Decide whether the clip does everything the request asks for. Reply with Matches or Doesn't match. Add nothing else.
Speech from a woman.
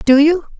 Matches